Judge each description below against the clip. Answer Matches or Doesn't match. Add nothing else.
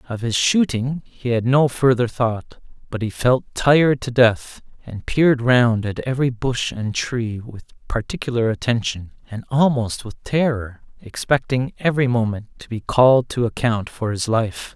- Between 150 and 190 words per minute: Matches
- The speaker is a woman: Doesn't match